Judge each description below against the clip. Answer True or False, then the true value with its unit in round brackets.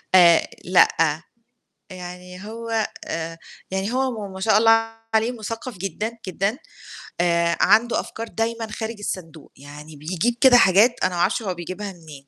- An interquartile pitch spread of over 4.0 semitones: True (4.7 semitones)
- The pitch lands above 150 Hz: True (190 Hz)